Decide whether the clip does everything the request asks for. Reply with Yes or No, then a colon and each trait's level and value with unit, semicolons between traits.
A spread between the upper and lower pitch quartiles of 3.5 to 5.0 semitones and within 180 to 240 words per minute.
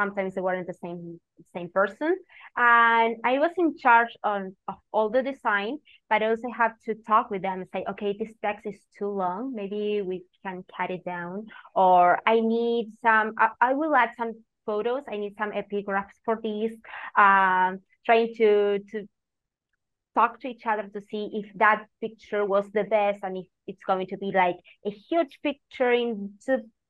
No: average, 2.8 semitones; average, 185 wpm